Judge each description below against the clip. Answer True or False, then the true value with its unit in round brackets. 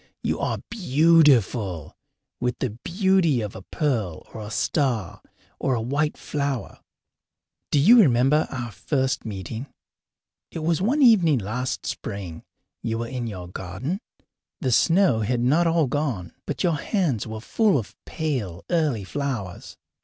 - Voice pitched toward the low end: True (130 Hz)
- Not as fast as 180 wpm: True (145 wpm)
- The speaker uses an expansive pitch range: True (6.3 semitones)